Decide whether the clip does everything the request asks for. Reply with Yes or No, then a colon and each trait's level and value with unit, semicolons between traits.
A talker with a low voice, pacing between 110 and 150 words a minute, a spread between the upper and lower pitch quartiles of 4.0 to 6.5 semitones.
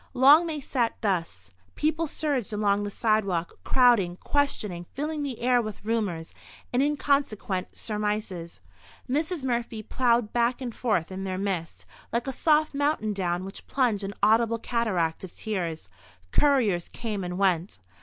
No: high, 220 Hz; average, 145 wpm; wide, 5.5 semitones